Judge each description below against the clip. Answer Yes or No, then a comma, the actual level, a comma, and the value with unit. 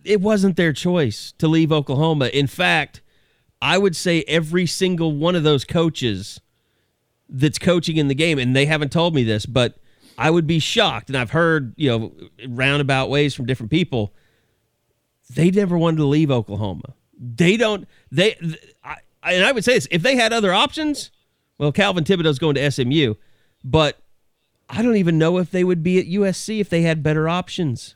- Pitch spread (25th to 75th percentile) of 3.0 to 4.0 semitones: No, average, 5.3 semitones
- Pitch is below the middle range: No, medium, 155 Hz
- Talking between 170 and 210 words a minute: Yes, average, 180 wpm